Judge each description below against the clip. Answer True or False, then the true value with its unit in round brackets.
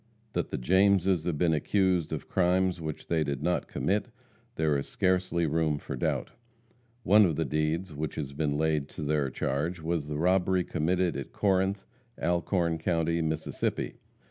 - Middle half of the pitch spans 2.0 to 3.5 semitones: True (3.1 semitones)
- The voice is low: True (85 Hz)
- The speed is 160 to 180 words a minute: True (165 wpm)